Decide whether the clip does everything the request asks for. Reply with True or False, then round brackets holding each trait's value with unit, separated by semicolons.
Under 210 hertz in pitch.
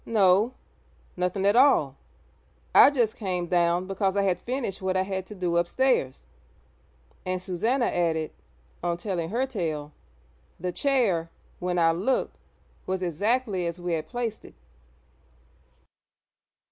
True (185 Hz)